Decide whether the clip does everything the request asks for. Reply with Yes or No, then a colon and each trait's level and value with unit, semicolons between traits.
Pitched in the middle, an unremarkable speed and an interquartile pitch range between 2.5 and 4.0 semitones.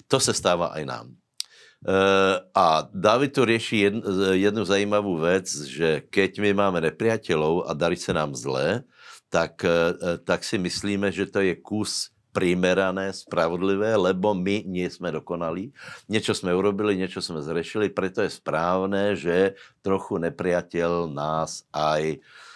No: very low, 95 Hz; average, 135 wpm; average, 2.8 semitones